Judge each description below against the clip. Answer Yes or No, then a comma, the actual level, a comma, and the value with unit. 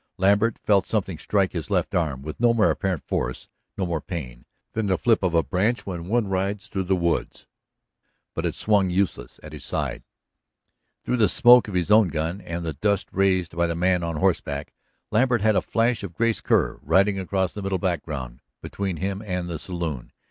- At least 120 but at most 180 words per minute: No, average, 200 wpm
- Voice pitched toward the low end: Yes, very low, 95 Hz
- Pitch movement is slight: No, average, 3.5 semitones